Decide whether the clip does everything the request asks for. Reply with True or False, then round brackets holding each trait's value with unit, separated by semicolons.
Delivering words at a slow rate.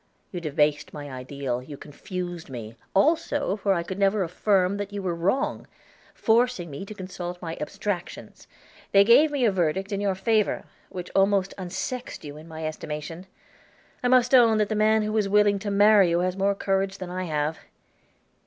False (175 wpm)